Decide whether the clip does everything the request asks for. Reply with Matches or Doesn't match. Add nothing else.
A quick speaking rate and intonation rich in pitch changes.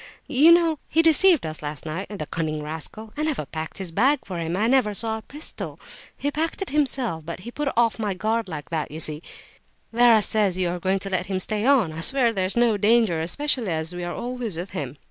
Matches